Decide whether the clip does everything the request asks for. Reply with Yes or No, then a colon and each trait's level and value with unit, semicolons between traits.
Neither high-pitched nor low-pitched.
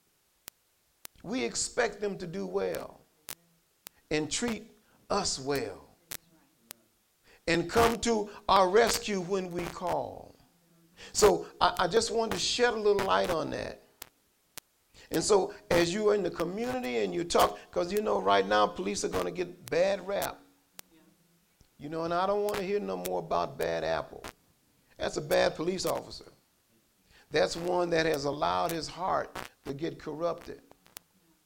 Yes: medium, 180 Hz